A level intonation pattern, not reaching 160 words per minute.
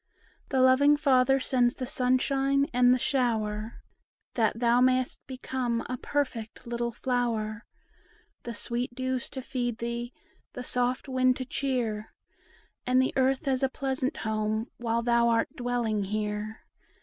Yes: narrow, 2.0 semitones; average, 140 wpm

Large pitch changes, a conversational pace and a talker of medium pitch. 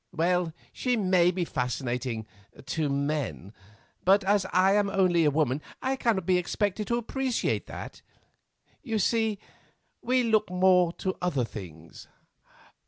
No: wide, 6.2 semitones; slow, 130 wpm; medium, 180 Hz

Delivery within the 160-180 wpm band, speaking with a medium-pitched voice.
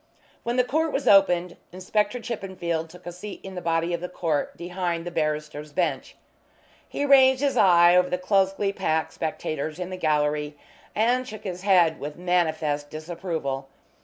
Yes: average, 165 wpm; medium, 175 Hz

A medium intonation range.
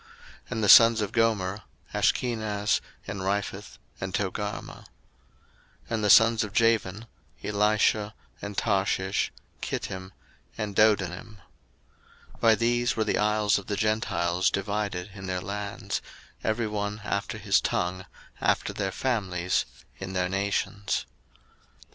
No: narrow, 2.1 semitones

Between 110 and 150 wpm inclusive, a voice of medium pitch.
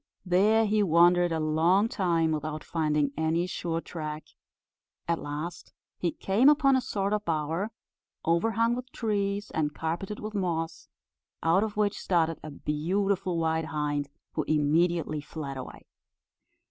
Yes: average, 140 wpm; medium, 170 Hz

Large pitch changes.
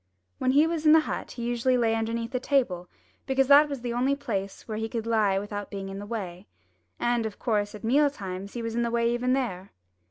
No: average, 3.9 semitones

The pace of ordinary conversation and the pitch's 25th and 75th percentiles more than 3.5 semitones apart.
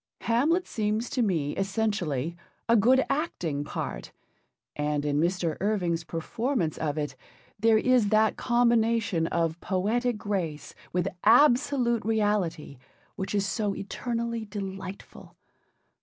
No: slow, 115 wpm; wide, 5.6 semitones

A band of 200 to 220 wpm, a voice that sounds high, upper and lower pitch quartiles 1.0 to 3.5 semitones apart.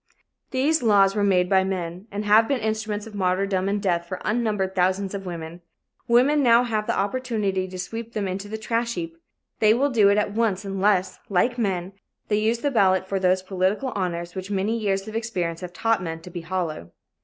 Yes: fast, 205 wpm; high, 200 Hz; average, 3.0 semitones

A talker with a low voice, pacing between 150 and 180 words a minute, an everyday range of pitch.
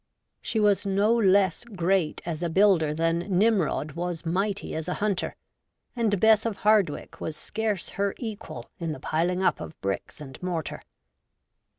No: medium, 185 Hz; average, 160 wpm; average, 4.0 semitones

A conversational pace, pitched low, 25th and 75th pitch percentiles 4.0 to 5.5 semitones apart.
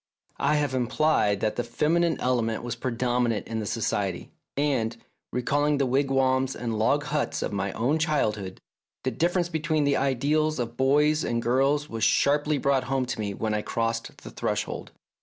Yes: average, 175 wpm; low, 130 Hz; average, 4.3 semitones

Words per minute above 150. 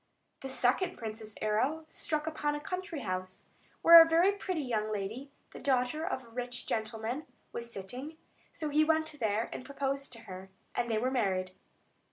Yes: average, 175 wpm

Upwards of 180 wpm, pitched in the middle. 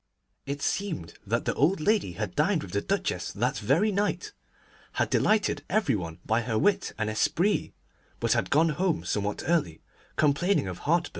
No: average, 170 wpm; medium, 150 Hz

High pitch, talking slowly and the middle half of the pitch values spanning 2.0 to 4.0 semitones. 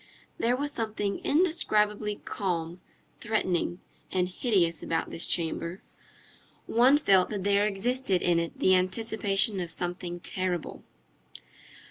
Yes: high, 195 Hz; slow, 115 wpm; average, 3.6 semitones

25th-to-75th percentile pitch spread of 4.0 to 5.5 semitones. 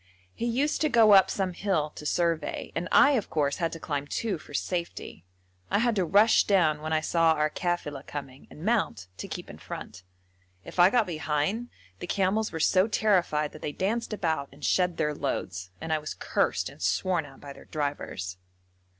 Yes: average, 5.2 semitones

